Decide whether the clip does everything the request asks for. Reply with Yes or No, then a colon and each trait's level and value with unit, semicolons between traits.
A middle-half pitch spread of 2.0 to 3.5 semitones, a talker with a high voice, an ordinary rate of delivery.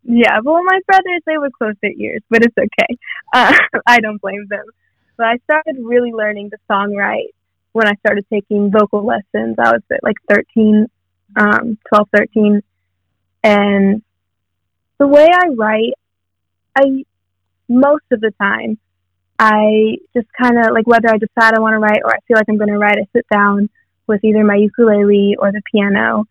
Yes: narrow, 2.6 semitones; high, 215 Hz; average, 180 wpm